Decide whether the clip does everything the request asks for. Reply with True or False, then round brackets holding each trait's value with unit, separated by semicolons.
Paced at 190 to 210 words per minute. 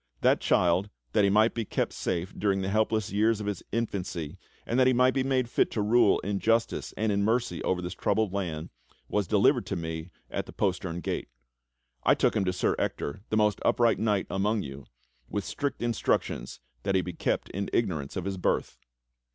True (200 wpm)